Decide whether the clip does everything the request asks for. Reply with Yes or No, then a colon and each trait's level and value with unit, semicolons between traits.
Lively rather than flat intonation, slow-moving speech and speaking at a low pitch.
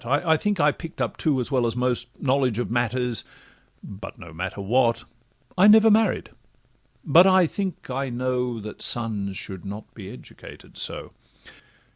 No: wide, 5.8 semitones; average, 150 wpm; low, 125 Hz